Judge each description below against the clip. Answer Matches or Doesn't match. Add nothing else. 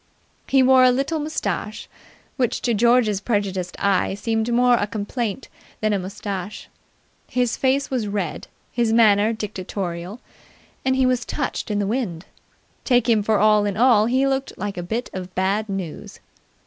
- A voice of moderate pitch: Doesn't match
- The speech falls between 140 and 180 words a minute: Matches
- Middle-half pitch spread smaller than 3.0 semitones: Doesn't match